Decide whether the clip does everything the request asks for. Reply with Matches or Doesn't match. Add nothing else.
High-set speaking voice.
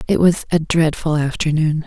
Doesn't match